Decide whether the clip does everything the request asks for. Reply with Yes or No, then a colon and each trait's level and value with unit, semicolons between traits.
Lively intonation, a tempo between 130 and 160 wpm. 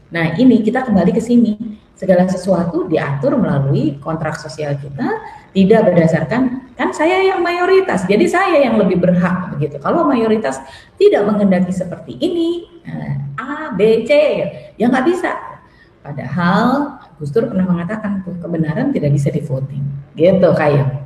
Yes: wide, 8.2 semitones; average, 135 wpm